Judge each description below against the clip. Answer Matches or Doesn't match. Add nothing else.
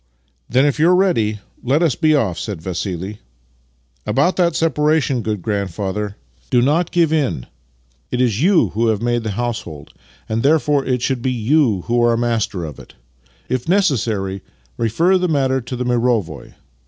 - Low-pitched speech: Matches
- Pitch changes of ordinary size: Doesn't match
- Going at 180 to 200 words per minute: Matches